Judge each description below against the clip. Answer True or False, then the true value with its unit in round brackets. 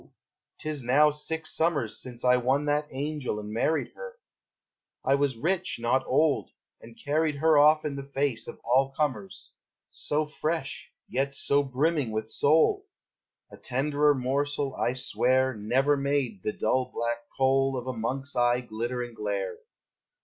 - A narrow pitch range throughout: False (3.3 semitones)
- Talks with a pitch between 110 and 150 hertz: True (135 Hz)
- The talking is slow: False (155 wpm)